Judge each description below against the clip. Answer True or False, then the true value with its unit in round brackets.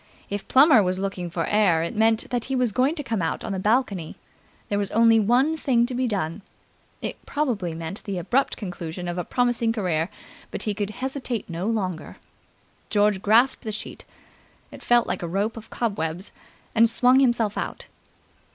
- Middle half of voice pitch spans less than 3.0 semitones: False (4.6 semitones)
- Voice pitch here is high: True (215 Hz)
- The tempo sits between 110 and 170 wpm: False (185 wpm)